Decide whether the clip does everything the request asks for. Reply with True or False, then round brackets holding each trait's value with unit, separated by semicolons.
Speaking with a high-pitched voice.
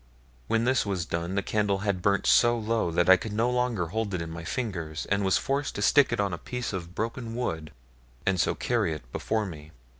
False (100 Hz)